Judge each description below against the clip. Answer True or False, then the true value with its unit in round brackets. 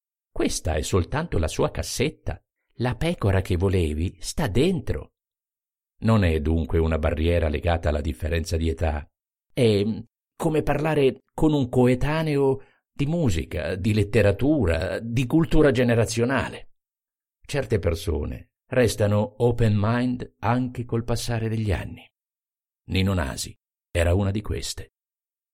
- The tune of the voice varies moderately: False (6.7 semitones)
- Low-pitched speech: True (105 Hz)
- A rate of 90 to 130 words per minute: True (120 wpm)